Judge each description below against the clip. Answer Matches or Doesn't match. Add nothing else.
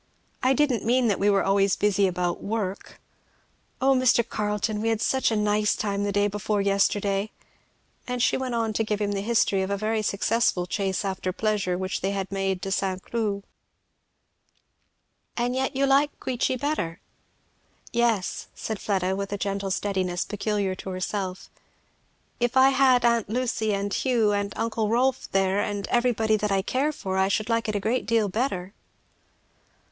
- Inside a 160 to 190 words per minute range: Matches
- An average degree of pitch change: Matches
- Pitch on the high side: Matches